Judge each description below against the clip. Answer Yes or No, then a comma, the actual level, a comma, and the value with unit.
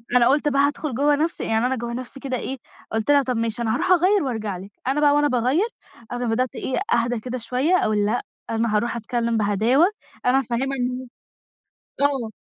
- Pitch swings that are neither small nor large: Yes, average, 3.2 semitones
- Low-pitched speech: No, very high, 250 Hz